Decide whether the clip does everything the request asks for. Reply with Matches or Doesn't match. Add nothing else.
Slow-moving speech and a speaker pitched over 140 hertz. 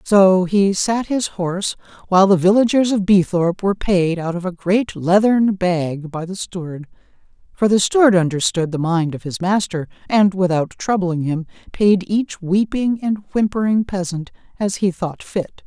Doesn't match